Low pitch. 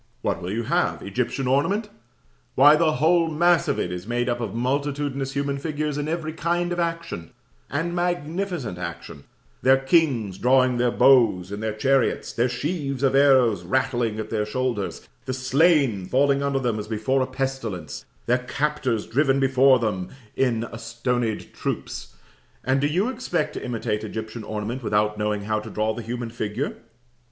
Yes: low, 130 Hz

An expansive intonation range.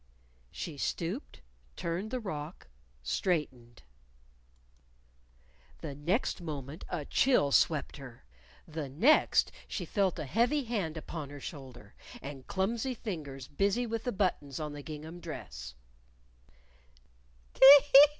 Yes: wide, 6.1 semitones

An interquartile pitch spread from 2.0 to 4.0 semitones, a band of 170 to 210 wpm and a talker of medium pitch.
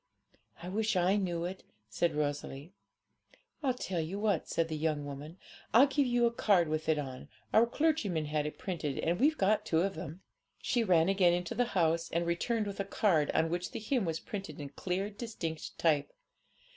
No: average, 4.7 semitones; average, 195 wpm; medium, 175 Hz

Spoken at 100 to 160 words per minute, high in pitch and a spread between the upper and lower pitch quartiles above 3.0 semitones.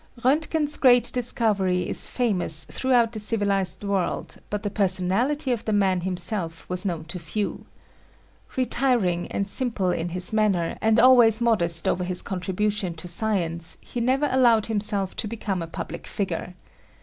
Yes: average, 155 wpm; high, 205 Hz; average, 4.4 semitones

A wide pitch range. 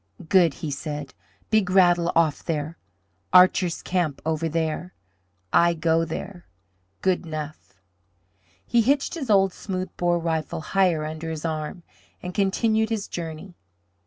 No: average, 3.0 semitones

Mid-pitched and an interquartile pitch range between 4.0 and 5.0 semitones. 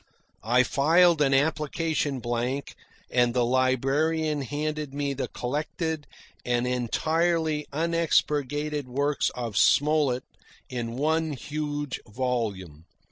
No: medium, 145 Hz; average, 3.5 semitones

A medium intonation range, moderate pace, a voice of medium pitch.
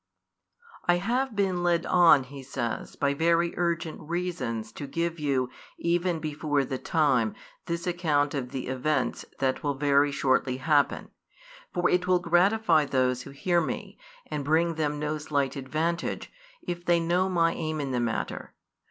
Yes: average, 3.8 semitones; average, 165 wpm; medium, 155 Hz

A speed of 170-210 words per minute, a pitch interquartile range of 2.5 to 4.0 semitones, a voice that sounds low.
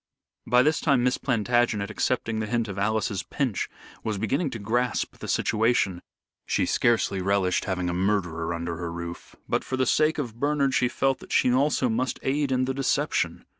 No: average, 185 wpm; average, 4.8 semitones; low, 115 Hz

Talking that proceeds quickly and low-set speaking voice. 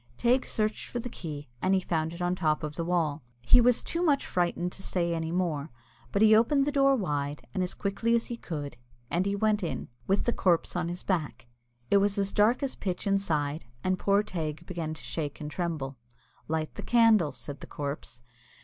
No: fast, 215 wpm; medium, 180 Hz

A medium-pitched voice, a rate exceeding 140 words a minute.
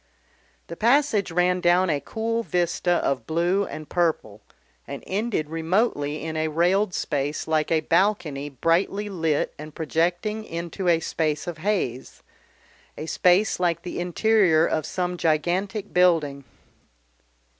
No: medium, 170 Hz; slow, 135 wpm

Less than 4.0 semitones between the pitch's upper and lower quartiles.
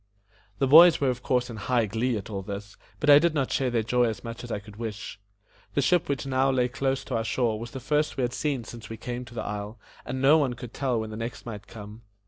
Yes: average, 3.2 semitones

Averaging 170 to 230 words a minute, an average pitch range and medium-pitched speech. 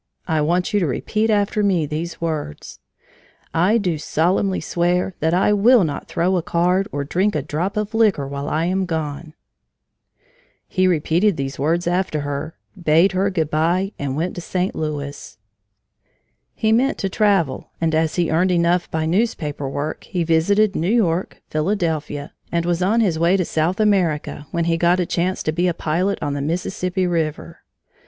Yes: average, 175 wpm; average, 3.3 semitones; medium, 170 Hz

